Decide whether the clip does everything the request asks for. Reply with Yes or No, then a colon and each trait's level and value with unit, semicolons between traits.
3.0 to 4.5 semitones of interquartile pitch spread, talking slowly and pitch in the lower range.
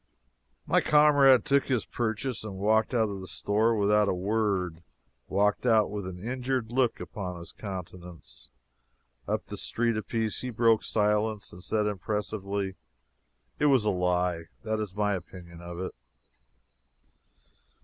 No: average, 3.4 semitones; average, 145 wpm; low, 105 Hz